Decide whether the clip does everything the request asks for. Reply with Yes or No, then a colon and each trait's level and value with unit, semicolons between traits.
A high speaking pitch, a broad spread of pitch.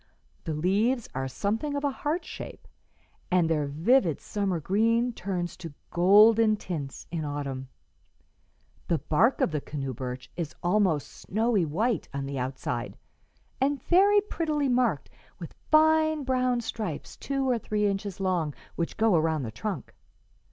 Yes: high, 200 Hz; wide, 8.0 semitones